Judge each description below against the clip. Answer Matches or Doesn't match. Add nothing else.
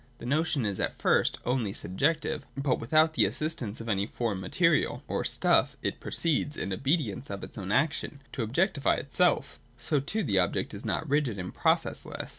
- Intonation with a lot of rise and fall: Matches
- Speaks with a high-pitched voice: Doesn't match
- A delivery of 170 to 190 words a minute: Matches